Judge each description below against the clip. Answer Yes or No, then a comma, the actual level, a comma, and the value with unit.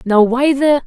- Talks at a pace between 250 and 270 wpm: No, fast, 210 wpm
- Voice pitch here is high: Yes, very high, 260 Hz